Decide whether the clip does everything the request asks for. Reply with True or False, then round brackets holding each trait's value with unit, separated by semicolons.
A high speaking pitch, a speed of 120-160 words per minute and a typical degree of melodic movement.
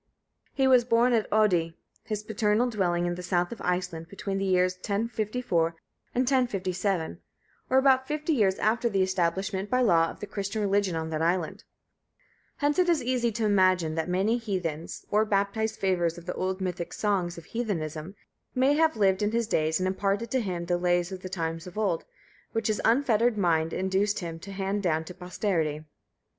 False (195 Hz; 185 wpm; 4.0 semitones)